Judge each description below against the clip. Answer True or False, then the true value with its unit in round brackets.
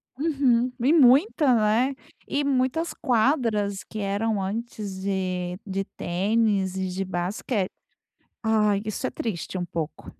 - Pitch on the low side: False (215 Hz)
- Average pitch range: True (4.7 semitones)